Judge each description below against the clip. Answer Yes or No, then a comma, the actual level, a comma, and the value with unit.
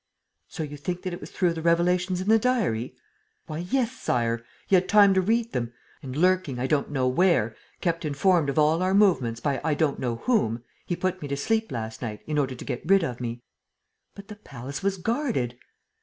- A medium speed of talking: No, fast, 215 wpm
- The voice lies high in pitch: No, medium, 165 Hz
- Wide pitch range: Yes, wide, 6.7 semitones